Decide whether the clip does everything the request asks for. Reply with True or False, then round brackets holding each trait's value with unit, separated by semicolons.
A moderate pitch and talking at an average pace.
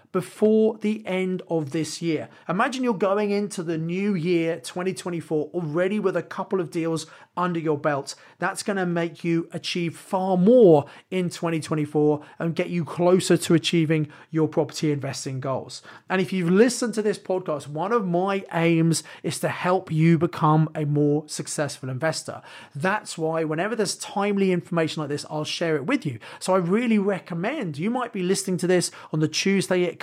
True (170 Hz; 180 wpm)